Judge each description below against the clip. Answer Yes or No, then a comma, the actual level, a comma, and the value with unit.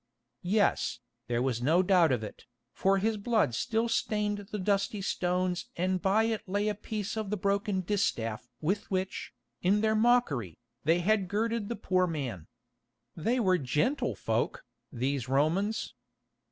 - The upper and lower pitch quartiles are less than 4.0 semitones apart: No, average, 5.1 semitones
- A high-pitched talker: Yes, high, 195 Hz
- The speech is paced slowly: No, average, 155 wpm